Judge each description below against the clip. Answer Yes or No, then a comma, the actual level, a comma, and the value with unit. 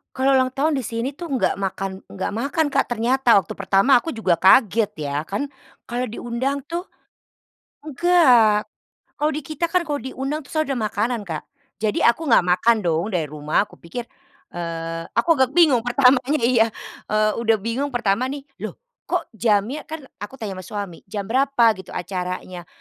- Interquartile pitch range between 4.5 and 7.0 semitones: Yes, wide, 5.6 semitones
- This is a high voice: Yes, high, 235 Hz